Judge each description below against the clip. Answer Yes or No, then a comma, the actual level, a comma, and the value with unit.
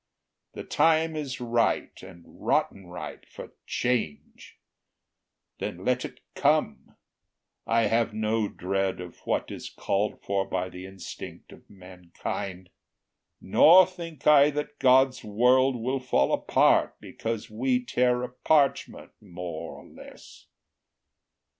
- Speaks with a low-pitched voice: Yes, low, 115 Hz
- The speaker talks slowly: Yes, slow, 120 wpm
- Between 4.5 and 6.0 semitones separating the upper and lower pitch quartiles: Yes, wide, 5.6 semitones